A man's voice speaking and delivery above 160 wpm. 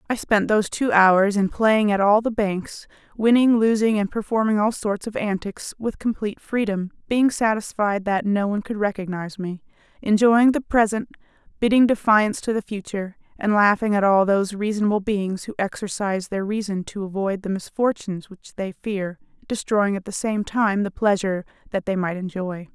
No: female; average, 175 wpm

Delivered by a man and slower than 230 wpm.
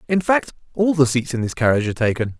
No: male; fast, 250 wpm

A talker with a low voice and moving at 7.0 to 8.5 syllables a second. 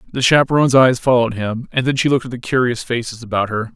Yes: low, 125 Hz; 7.1 syllables/s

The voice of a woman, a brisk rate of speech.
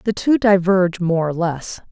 No: female; average, 190 wpm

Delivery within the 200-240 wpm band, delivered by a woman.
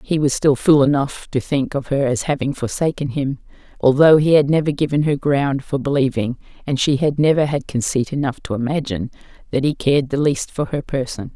Yes: fast, 205 wpm; female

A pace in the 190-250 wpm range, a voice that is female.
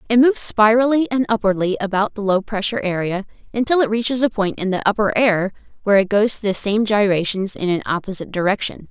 Yes: average, 200 wpm; female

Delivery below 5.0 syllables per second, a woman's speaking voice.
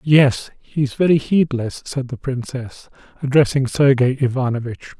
No: 4.5 syllables/s; male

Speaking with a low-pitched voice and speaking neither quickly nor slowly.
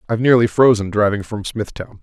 Yes: low, 110 Hz; average, 180 wpm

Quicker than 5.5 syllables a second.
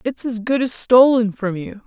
No: 4.5 syllables/s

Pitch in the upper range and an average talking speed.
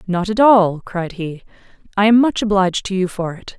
No: high, 195 Hz; fast, 220 wpm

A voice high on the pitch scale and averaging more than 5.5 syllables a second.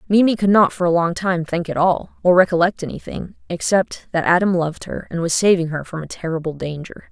No: medium, 175 Hz; 5.8 syllables/s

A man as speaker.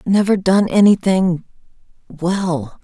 No: female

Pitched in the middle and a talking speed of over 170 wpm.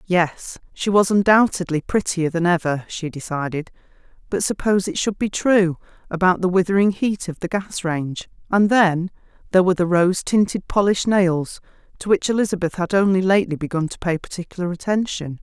No: medium, 180 Hz; average, 165 wpm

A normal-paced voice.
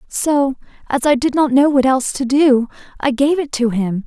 No: fast, 220 wpm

